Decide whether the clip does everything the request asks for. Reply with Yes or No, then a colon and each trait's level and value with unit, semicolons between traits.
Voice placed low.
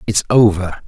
Yes: low, 100 Hz